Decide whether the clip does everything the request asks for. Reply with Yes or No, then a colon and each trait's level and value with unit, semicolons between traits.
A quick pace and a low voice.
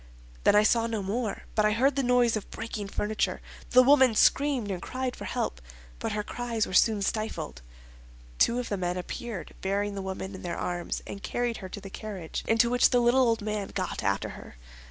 No: fast, 210 wpm; high, 215 Hz